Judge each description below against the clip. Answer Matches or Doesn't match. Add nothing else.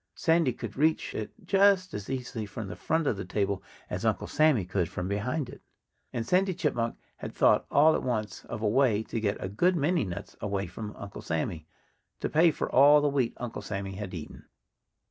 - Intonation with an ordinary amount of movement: Doesn't match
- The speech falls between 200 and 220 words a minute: Matches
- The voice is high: Doesn't match